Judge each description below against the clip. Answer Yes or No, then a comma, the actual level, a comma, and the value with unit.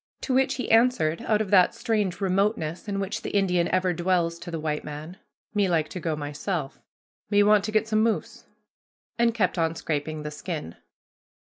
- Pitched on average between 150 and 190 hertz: Yes, medium, 185 Hz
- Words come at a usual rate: Yes, average, 190 wpm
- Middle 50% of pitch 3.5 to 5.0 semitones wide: Yes, average, 4.7 semitones